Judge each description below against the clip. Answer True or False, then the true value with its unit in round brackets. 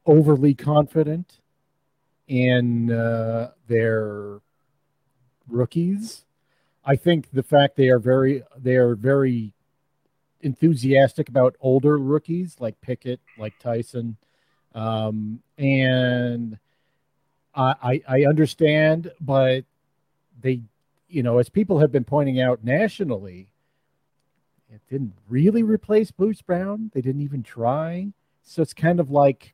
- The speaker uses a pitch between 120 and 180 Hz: True (135 Hz)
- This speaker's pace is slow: True (115 wpm)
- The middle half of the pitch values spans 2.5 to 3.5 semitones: False (4.0 semitones)